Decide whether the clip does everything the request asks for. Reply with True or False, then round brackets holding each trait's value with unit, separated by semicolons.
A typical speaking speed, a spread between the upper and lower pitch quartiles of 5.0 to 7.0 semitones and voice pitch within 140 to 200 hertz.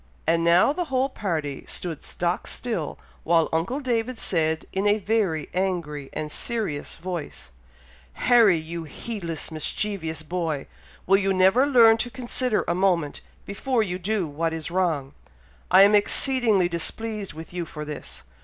True (150 wpm; 5.4 semitones; 185 Hz)